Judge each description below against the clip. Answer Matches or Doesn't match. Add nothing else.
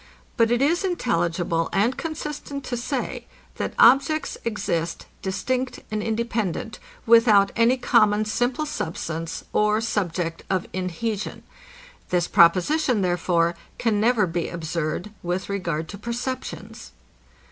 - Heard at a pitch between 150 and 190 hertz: Doesn't match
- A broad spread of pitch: Matches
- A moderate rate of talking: Doesn't match